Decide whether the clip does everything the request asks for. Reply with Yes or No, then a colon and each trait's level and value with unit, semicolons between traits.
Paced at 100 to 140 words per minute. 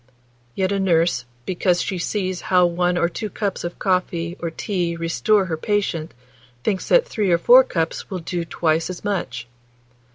No: average, 170 wpm